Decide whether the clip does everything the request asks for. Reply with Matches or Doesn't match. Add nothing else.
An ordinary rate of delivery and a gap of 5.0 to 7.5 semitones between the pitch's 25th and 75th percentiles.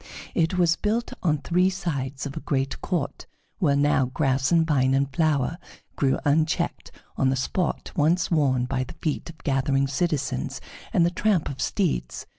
Doesn't match